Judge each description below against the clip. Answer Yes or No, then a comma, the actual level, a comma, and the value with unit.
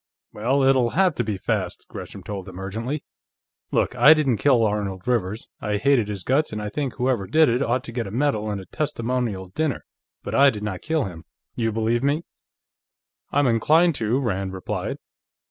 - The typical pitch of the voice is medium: No, low, 115 Hz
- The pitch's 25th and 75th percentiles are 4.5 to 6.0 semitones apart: Yes, average, 5.0 semitones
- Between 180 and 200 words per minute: Yes, average, 190 wpm